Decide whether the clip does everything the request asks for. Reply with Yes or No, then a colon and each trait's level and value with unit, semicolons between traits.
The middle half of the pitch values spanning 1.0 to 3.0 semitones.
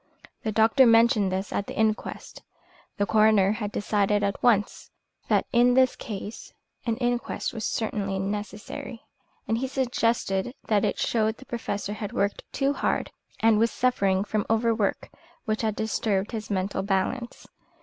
Yes: narrow, 2.4 semitones